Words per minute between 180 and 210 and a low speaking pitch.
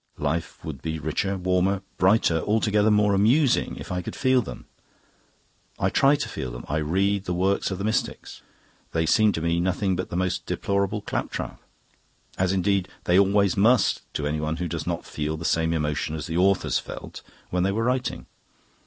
Yes: average, 185 wpm; very low, 95 Hz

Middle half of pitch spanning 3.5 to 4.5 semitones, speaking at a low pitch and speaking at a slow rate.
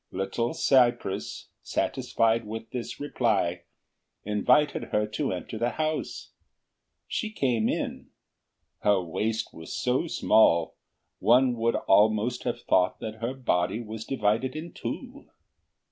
No: average, 3.1 semitones; low, 115 Hz; slow, 120 wpm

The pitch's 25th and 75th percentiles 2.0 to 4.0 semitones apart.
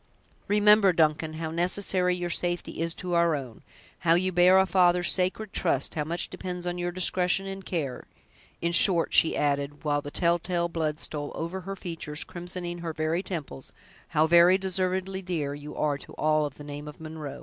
Yes: average, 2.9 semitones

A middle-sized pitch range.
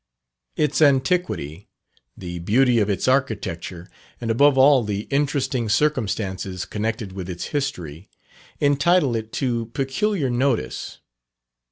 No: wide, 6.0 semitones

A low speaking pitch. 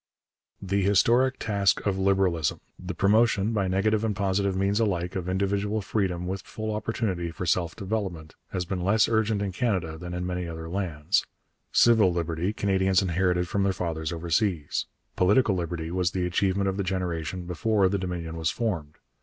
Yes: very low, 95 Hz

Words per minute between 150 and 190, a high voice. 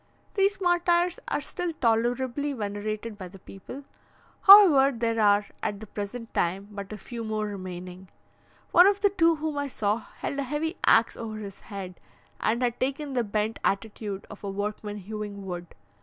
Yes: average, 170 wpm; high, 220 Hz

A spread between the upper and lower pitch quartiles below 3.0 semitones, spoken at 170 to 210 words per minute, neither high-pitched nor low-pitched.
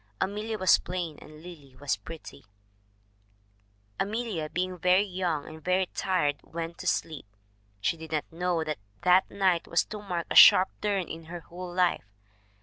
No: narrow, 2.6 semitones; average, 160 wpm; medium, 175 Hz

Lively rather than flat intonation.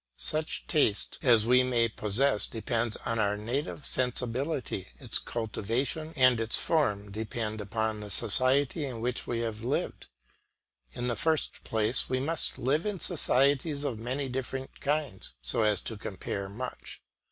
No: average, 4.0 semitones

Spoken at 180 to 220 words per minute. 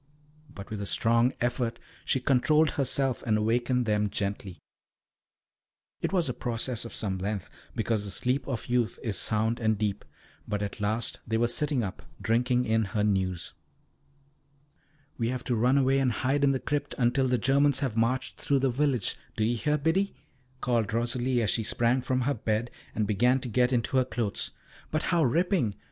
Yes: average, 185 wpm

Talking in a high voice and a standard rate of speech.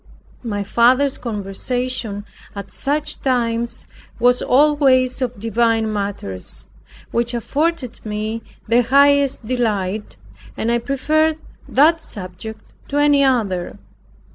No: high, 240 Hz; slow, 105 wpm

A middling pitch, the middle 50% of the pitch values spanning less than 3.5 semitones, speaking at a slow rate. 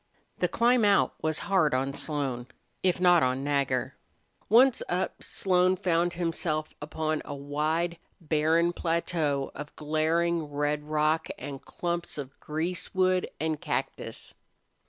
Yes: medium, 160 Hz; average, 3.0 semitones; slow, 125 wpm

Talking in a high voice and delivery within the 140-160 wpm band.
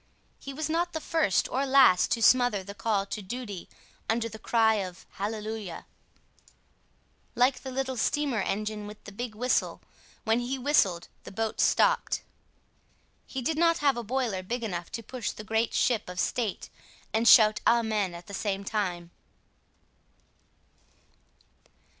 Yes: high, 225 Hz; average, 150 wpm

